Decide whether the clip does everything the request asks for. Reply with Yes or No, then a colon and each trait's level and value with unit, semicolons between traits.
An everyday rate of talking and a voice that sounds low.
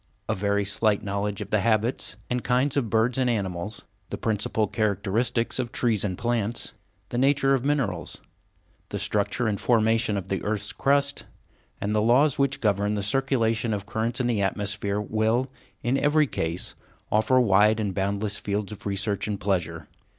Yes: average, 170 wpm; low, 110 Hz